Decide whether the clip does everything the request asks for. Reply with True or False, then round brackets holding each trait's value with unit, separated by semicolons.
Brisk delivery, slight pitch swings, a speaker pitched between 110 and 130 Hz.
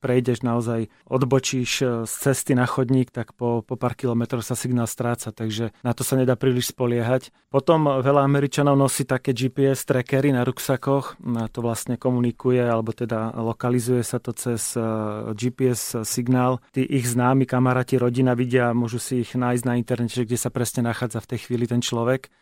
True (170 wpm; 1.6 semitones; 125 Hz)